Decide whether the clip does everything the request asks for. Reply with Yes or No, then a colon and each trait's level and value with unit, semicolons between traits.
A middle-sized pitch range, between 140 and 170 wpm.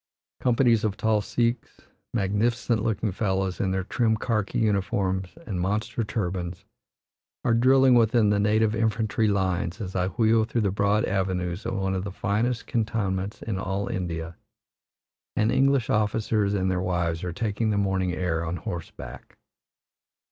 Yes: average, 3.0 semitones; average, 150 wpm